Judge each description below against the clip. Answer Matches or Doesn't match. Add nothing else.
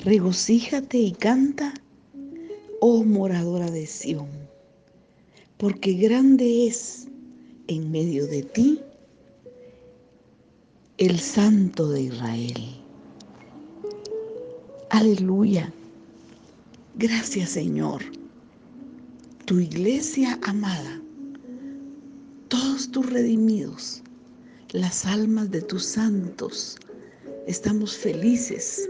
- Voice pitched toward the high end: Matches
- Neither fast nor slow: Doesn't match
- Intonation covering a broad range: Matches